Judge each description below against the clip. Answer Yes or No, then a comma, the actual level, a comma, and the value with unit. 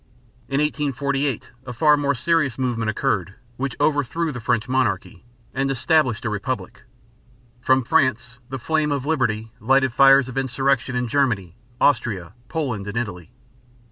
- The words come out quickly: No, average, 140 wpm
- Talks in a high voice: No, low, 130 Hz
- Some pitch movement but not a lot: Yes, average, 3.5 semitones